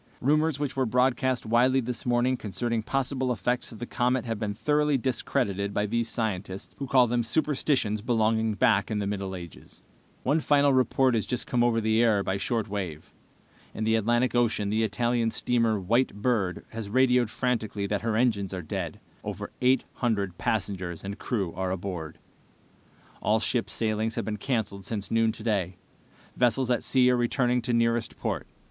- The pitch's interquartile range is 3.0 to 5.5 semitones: Yes, average, 3.4 semitones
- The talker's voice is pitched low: Yes, low, 115 Hz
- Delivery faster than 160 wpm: Yes, average, 175 wpm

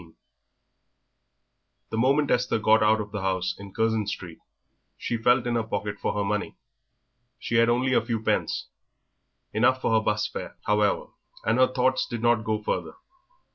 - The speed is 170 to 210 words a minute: Yes, average, 175 wpm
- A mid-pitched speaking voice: No, low, 110 Hz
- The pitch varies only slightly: Yes, narrow, 2.3 semitones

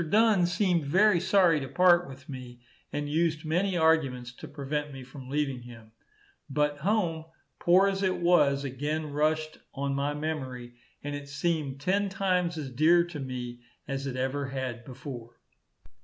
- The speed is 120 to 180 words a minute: Yes, average, 160 wpm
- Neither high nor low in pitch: Yes, medium, 150 Hz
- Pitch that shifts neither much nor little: Yes, average, 4.5 semitones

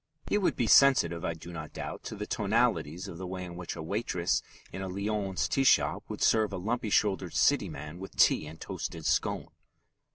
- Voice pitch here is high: No, very low, 95 Hz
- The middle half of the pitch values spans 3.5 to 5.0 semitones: Yes, average, 4.0 semitones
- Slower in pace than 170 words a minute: No, fast, 205 wpm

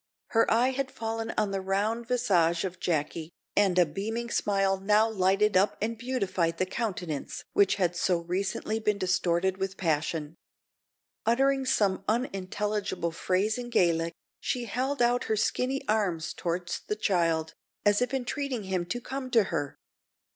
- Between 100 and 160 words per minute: Yes, average, 155 wpm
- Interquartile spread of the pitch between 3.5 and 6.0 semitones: Yes, average, 4.4 semitones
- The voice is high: Yes, high, 200 Hz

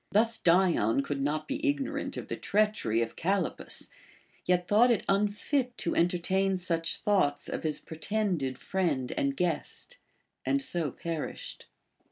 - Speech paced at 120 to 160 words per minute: Yes, average, 140 wpm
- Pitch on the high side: No, medium, 180 Hz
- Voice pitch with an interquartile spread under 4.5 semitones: No, average, 5.3 semitones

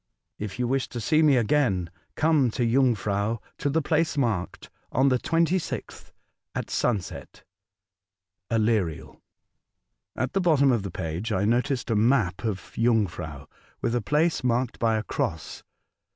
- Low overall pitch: Yes, low, 120 Hz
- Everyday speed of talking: Yes, average, 145 wpm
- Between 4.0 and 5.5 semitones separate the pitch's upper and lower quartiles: Yes, average, 5.1 semitones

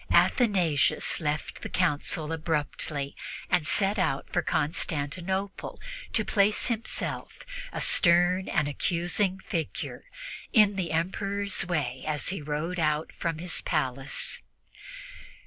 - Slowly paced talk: Yes, slow, 110 wpm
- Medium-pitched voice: Yes, medium, 170 Hz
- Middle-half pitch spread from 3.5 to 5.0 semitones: Yes, average, 4.2 semitones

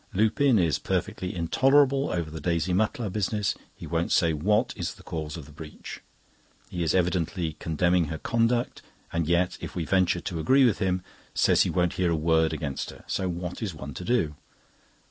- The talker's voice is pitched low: Yes, very low, 90 Hz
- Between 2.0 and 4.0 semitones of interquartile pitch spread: No, average, 4.5 semitones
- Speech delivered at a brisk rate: No, average, 190 wpm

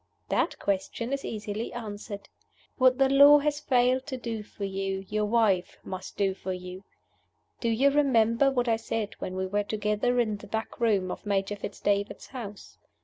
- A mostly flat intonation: No, average, 3.7 semitones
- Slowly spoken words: No, average, 180 wpm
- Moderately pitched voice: No, high, 215 Hz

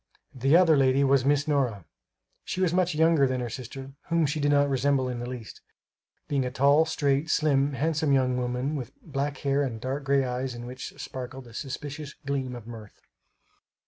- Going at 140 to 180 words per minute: No, average, 190 wpm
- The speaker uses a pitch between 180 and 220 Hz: No, low, 135 Hz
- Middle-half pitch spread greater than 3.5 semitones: No, narrow, 2.4 semitones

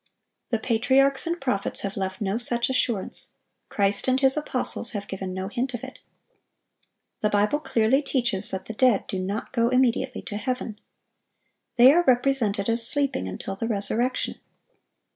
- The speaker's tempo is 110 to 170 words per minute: Yes, average, 160 wpm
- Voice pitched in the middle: No, high, 235 Hz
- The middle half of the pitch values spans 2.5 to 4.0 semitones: No, average, 4.5 semitones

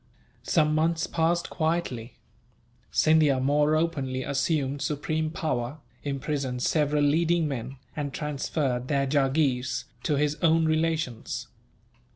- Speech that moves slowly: Yes, slow, 110 wpm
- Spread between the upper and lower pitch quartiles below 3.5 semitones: Yes, average, 2.9 semitones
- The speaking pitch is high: No, medium, 150 Hz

